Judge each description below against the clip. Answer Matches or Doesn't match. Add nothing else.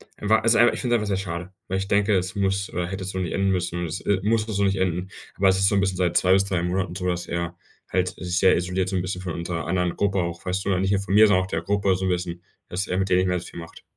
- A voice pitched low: Matches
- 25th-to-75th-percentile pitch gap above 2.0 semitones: Doesn't match